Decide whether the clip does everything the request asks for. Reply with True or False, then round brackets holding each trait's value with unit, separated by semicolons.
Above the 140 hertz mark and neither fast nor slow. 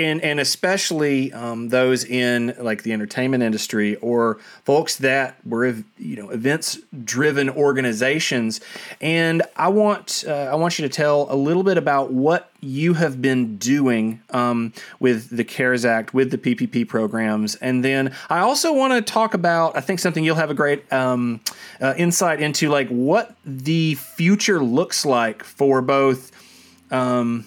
False (135 Hz; 160 wpm)